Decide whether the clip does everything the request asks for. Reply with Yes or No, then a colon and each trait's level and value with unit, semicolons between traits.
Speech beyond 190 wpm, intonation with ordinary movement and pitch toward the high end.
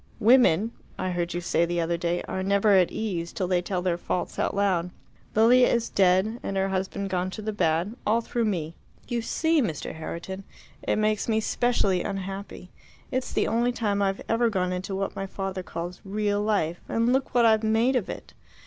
Yes: average, 200 wpm; average, 3.5 semitones; high, 195 Hz